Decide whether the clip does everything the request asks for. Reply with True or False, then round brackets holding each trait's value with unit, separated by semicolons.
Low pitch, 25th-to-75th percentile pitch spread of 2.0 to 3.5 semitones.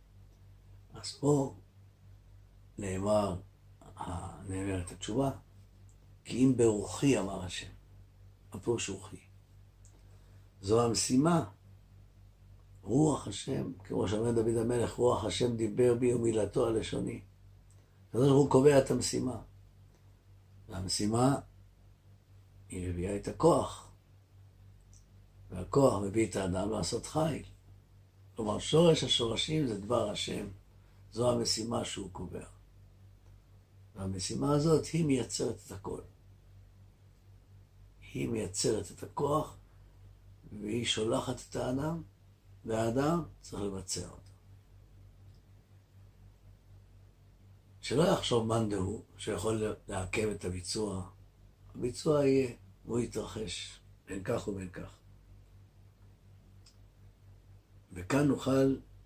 True (100 Hz; 2.4 semitones)